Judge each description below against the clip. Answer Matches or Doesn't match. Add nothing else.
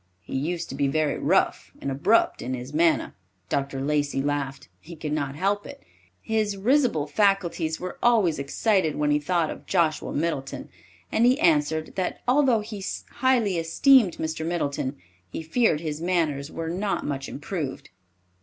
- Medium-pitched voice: Matches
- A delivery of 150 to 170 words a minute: Matches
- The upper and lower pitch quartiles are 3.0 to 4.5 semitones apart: Doesn't match